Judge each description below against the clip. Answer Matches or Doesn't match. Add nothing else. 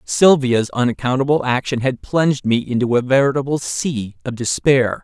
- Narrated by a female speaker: Doesn't match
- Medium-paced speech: Matches